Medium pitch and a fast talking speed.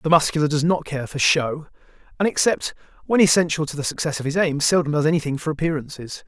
Yes: medium, 155 Hz; fast, 210 wpm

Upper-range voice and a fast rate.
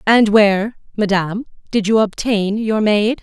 No: high, 210 Hz; average, 150 wpm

